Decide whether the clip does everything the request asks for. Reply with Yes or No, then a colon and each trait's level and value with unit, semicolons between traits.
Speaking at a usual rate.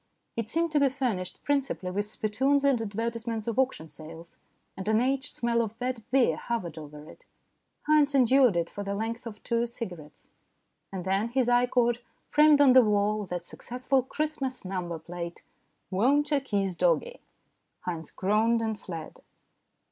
Yes: average, 165 wpm